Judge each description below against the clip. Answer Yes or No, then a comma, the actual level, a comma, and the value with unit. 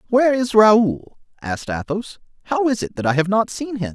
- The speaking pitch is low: No, high, 200 Hz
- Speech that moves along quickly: Yes, fast, 215 wpm